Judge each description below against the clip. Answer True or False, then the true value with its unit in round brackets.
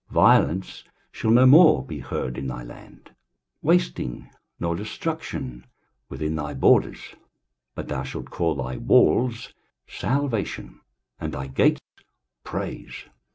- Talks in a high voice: False (85 Hz)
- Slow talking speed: True (120 wpm)